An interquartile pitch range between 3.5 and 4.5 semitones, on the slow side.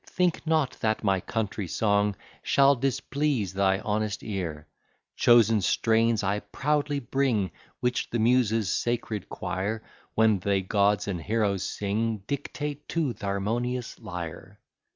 Yes: average, 3.9 semitones; slow, 130 wpm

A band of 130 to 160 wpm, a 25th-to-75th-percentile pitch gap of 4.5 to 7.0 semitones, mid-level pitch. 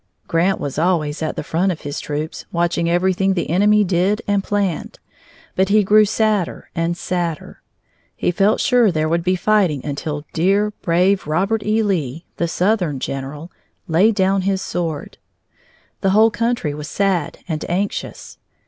No: average, 155 wpm; average, 3.8 semitones; medium, 180 Hz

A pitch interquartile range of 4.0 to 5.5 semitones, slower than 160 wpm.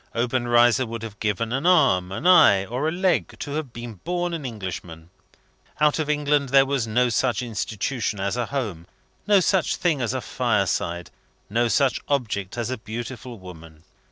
No: average, 5.2 semitones; average, 175 wpm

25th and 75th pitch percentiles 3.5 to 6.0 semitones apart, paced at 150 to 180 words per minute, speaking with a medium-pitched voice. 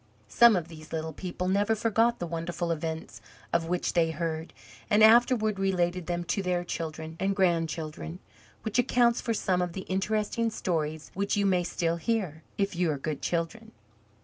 Yes: average, 3.9 semitones; average, 175 wpm; medium, 180 Hz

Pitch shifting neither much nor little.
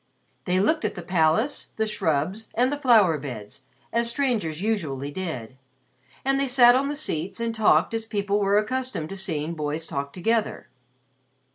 No: wide, 6.8 semitones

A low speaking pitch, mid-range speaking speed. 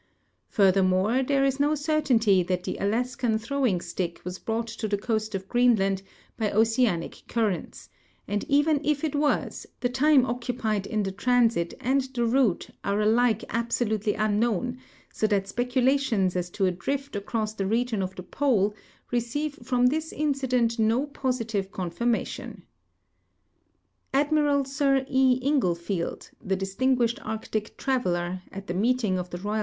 No: high, 230 Hz; average, 150 wpm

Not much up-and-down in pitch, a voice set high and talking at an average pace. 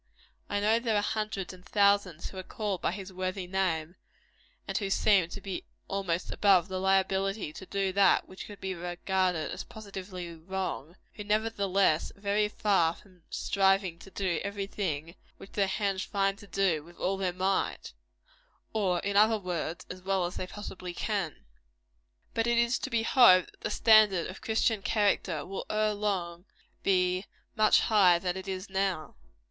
Yes: narrow, 2.1 semitones; high, 195 Hz; average, 175 wpm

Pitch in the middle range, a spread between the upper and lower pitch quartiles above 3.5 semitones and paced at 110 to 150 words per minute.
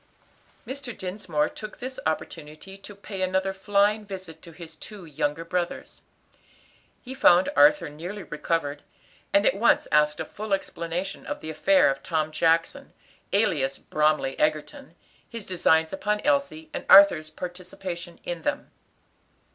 Yes: medium, 175 Hz; average, 4.3 semitones; average, 140 wpm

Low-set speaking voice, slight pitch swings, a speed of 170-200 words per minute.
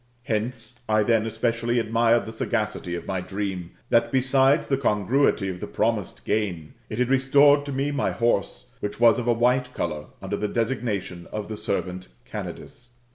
No: low, 115 Hz; average, 3.7 semitones; average, 175 wpm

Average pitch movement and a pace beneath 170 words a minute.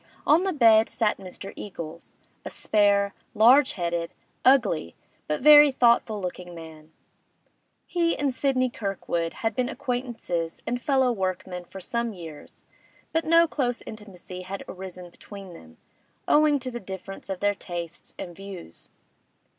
No: wide, 5.9 semitones; average, 140 wpm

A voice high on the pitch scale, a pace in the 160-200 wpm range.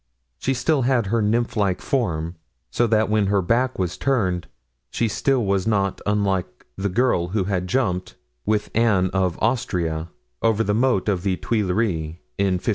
No: low, 100 Hz; average, 170 wpm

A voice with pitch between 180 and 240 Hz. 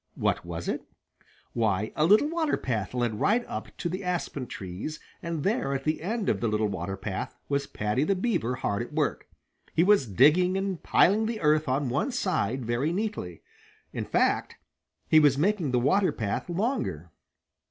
No: medium, 150 Hz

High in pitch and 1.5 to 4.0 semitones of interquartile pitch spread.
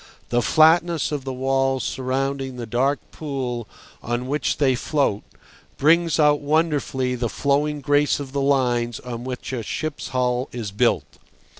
No: low, 135 Hz; average, 2.9 semitones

